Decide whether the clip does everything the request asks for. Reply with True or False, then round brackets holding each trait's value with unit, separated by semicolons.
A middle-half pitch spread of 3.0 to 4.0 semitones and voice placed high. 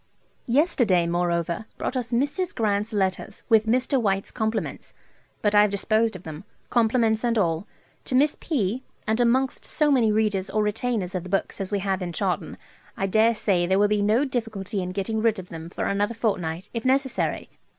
True (3.5 semitones; 215 Hz)